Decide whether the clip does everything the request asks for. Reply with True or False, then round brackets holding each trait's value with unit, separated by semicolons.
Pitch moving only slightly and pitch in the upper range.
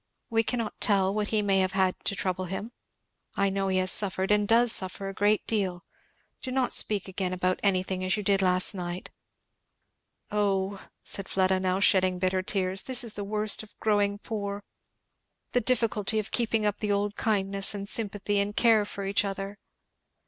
True (1.8 semitones; 200 Hz)